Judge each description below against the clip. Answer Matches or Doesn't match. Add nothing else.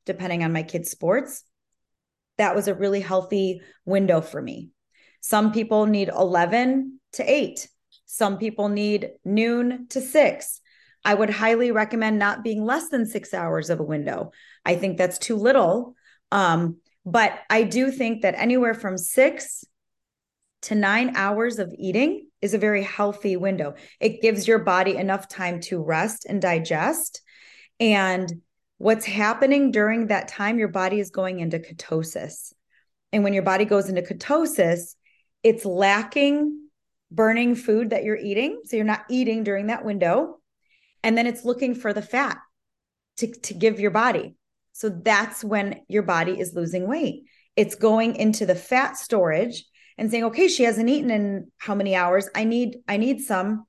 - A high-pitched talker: Matches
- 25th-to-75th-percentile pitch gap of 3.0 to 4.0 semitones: Matches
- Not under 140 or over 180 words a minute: Matches